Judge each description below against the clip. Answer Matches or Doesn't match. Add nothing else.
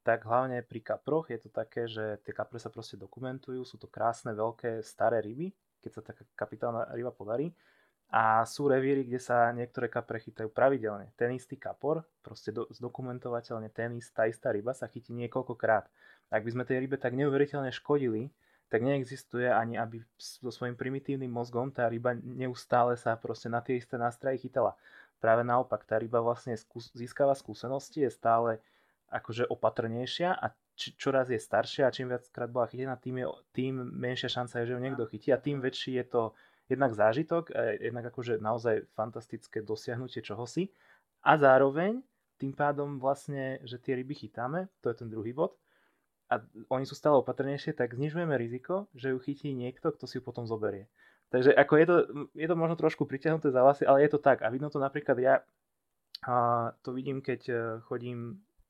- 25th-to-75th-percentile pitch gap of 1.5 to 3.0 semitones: Matches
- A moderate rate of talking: Doesn't match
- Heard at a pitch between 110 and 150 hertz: Matches